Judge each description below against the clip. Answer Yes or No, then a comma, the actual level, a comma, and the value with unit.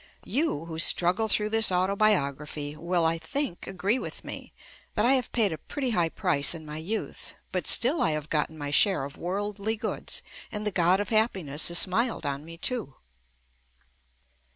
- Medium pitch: Yes, medium, 180 Hz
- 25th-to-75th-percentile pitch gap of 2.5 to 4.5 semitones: No, wide, 5.4 semitones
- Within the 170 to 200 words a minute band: Yes, average, 175 wpm